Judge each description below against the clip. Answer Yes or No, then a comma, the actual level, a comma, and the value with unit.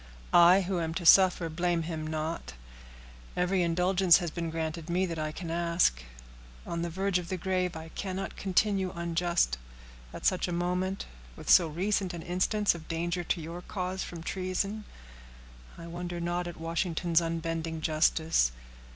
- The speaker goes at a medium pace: Yes, average, 160 wpm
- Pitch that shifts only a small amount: Yes, narrow, 1.8 semitones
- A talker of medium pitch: Yes, medium, 175 Hz